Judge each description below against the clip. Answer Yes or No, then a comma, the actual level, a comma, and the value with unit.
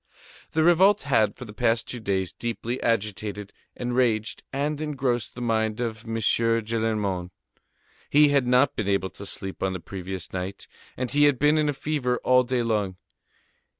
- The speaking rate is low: No, average, 170 wpm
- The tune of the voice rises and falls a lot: No, average, 3.8 semitones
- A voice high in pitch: No, low, 115 Hz